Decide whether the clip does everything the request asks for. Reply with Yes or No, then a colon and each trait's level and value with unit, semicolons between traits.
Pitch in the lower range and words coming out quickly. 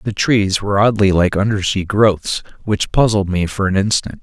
No: low, 100 Hz; average, 185 wpm